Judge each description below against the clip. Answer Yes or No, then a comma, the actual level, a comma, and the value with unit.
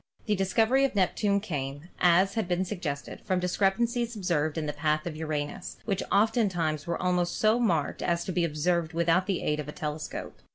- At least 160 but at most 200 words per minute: Yes, average, 195 wpm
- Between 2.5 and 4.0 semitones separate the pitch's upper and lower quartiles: No, average, 4.4 semitones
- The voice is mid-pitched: Yes, medium, 175 Hz